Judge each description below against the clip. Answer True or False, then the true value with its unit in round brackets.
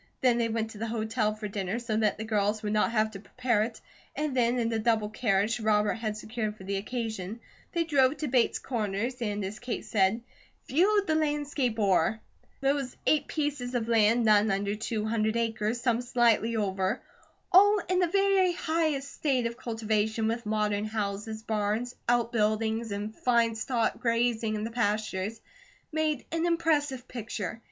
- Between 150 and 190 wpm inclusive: True (175 wpm)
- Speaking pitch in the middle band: False (225 Hz)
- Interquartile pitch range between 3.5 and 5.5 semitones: False (2.9 semitones)